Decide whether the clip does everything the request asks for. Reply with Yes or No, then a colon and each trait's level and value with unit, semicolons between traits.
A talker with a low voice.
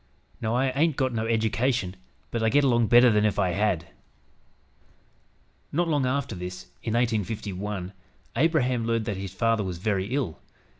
Yes: low, 115 Hz